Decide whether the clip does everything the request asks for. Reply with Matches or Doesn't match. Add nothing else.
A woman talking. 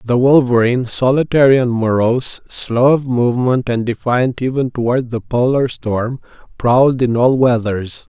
Doesn't match